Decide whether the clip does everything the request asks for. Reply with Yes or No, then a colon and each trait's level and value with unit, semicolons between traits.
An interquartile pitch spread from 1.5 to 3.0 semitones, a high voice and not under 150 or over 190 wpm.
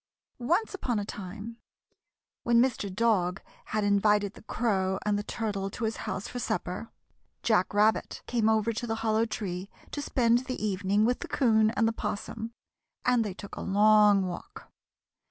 Yes: narrow, 2.4 semitones; high, 215 Hz; average, 170 wpm